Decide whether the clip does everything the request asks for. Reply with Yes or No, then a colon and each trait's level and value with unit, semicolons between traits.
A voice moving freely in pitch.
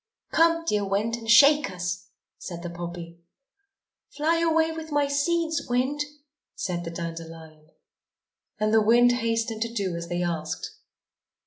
Yes: wide, 8.9 semitones